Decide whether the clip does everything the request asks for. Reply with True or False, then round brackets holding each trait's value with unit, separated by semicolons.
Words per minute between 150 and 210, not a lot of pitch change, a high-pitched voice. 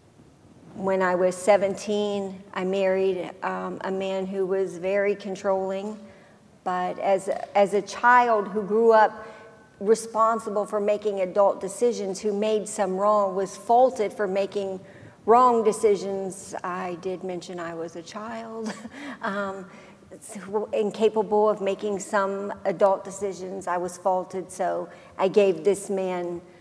False (135 wpm; 1.9 semitones; 195 Hz)